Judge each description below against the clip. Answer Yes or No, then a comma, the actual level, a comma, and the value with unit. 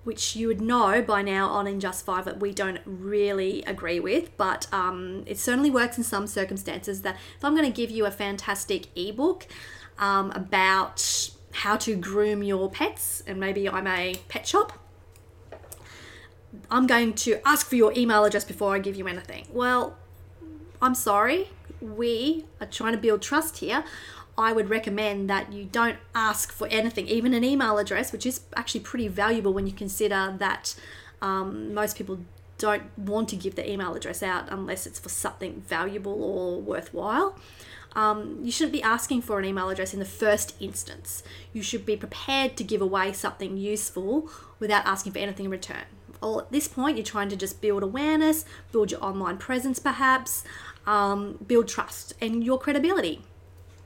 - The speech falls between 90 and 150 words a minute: No, average, 175 wpm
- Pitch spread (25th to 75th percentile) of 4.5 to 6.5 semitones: No, average, 3.4 semitones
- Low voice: No, high, 205 Hz